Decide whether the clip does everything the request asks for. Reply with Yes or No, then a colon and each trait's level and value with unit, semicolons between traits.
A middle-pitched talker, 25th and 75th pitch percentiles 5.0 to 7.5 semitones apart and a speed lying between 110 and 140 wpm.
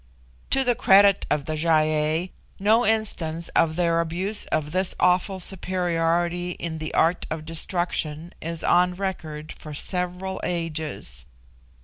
No: medium, 170 Hz; average, 2.8 semitones; slow, 135 wpm